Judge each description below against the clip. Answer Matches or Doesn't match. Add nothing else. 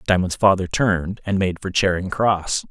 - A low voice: Matches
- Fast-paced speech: Doesn't match